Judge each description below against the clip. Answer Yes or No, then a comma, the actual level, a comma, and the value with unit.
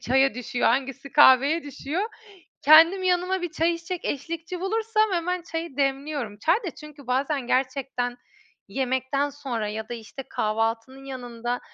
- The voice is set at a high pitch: Yes, very high, 275 Hz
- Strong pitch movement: No, average, 5.0 semitones